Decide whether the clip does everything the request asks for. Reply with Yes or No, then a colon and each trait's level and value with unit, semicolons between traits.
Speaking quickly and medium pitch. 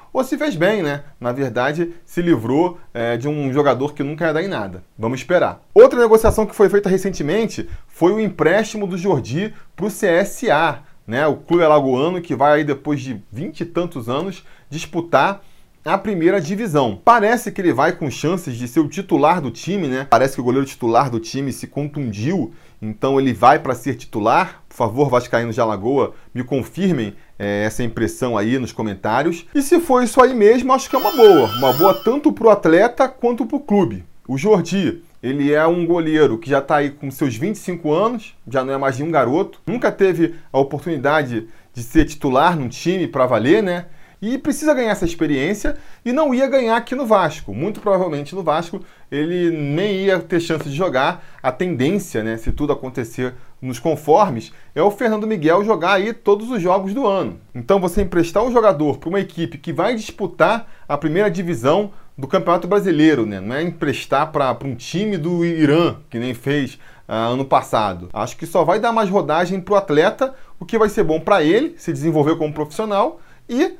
Yes: fast, 200 wpm; medium, 165 Hz